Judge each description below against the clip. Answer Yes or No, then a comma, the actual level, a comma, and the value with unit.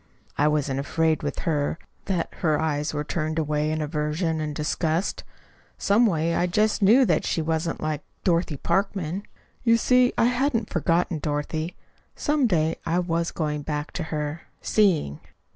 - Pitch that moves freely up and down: No, average, 3.4 semitones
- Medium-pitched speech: Yes, medium, 160 Hz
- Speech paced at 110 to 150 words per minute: No, average, 160 wpm